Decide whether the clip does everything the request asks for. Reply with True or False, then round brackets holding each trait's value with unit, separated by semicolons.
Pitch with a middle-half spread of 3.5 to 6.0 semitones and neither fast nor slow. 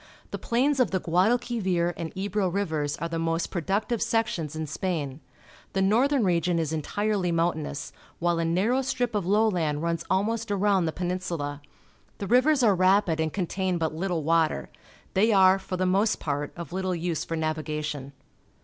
True (4.0 semitones; 170 wpm)